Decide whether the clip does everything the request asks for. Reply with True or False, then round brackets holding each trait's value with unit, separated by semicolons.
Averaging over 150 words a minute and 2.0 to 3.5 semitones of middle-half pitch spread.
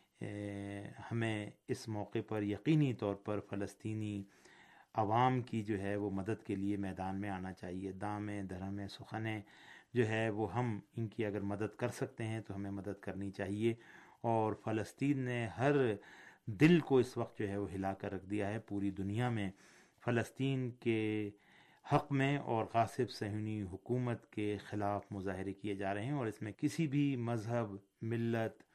True (165 wpm; 2.8 semitones)